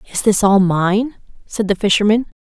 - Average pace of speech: Yes, average, 175 wpm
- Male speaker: No, female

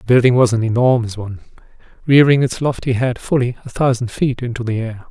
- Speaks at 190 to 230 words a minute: Yes, average, 200 wpm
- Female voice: No, male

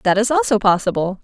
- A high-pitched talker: Yes, high, 200 Hz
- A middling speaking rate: Yes, average, 195 wpm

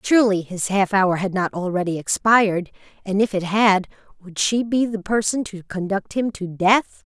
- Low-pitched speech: No, high, 200 Hz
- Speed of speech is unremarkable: Yes, average, 185 wpm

